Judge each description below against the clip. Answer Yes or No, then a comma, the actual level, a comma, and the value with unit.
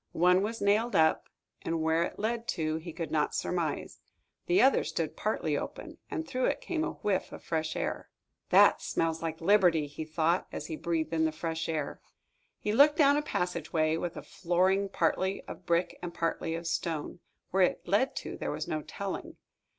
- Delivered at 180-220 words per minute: Yes, average, 190 wpm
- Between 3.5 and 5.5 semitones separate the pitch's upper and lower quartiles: Yes, average, 3.8 semitones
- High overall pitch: No, medium, 170 Hz